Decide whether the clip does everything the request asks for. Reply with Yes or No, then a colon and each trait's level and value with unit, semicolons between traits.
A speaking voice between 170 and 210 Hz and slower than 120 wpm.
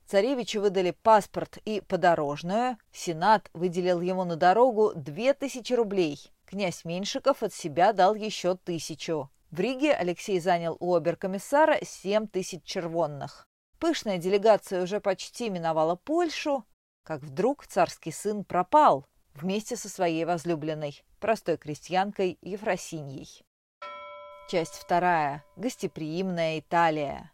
Yes: medium, 185 Hz; slow, 110 wpm